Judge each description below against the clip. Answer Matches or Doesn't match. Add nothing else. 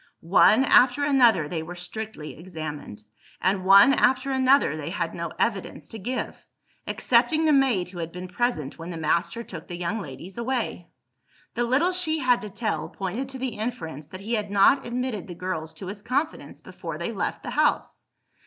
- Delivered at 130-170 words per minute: Doesn't match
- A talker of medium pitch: Doesn't match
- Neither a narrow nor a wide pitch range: Doesn't match